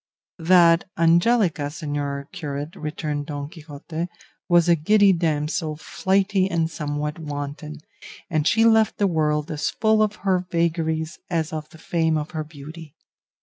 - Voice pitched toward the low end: No, medium, 160 Hz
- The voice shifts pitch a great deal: No, average, 2.9 semitones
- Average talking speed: Yes, average, 145 wpm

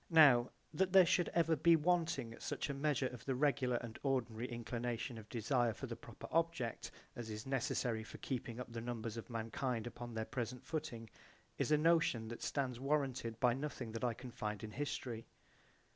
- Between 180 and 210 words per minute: Yes, average, 190 wpm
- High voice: No, low, 125 Hz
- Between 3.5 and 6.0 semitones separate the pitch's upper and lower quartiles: Yes, average, 3.9 semitones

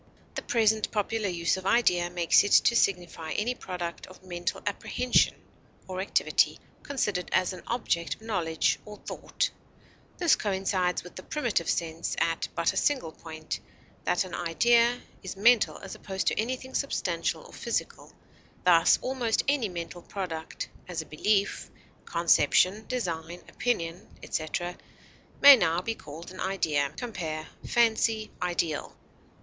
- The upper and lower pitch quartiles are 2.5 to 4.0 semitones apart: No, average, 4.9 semitones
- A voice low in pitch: No, medium, 185 Hz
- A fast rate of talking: No, average, 140 wpm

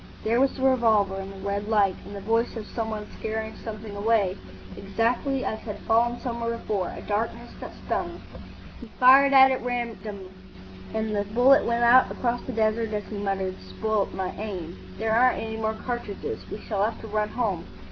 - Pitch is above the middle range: Yes, high, 220 Hz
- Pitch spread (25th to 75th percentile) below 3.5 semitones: Yes, average, 2.7 semitones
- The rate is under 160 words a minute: No, average, 185 wpm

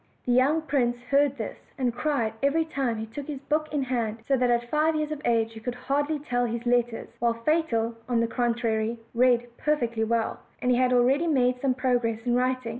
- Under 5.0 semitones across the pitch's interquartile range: Yes, average, 3.1 semitones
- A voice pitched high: Yes, very high, 250 Hz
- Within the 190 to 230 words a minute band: Yes, fast, 205 wpm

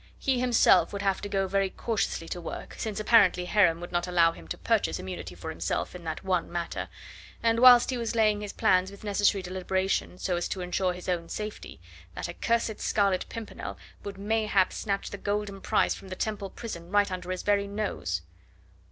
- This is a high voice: Yes, high, 195 Hz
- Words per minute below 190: No, average, 195 wpm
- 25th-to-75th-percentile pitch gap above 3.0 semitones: No, average, 2.7 semitones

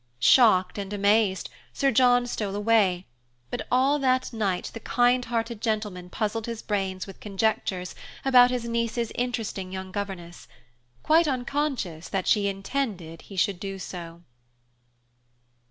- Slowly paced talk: Yes, slow, 130 wpm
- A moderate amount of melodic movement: Yes, average, 4.3 semitones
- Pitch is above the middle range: Yes, high, 210 Hz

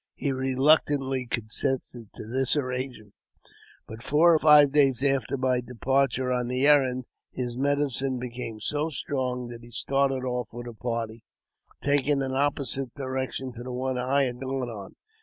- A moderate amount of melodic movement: No, narrow, 2.0 semitones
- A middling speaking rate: Yes, average, 160 wpm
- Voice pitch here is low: Yes, low, 130 Hz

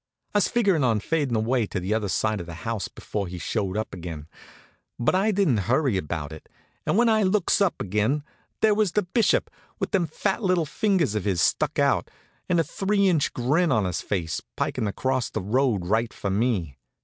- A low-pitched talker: Yes, low, 120 Hz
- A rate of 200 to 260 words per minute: Yes, fast, 205 wpm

